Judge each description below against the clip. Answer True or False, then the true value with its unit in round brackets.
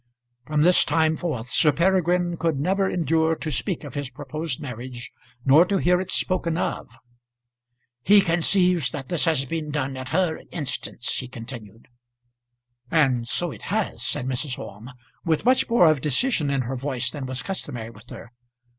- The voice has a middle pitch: True (150 Hz)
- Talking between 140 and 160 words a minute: False (170 wpm)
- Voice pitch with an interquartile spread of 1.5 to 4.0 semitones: False (5.1 semitones)